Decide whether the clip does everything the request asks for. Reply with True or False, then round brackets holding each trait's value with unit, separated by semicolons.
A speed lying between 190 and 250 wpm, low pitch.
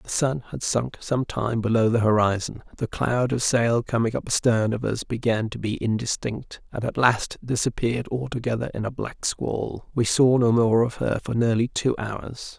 True (195 wpm; 115 Hz)